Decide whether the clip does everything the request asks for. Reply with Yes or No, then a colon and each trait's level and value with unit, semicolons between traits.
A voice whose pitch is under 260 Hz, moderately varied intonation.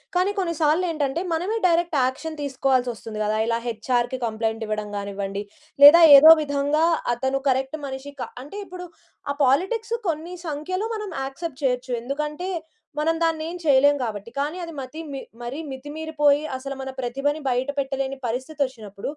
No: very high, 275 Hz; average, 4.0 semitones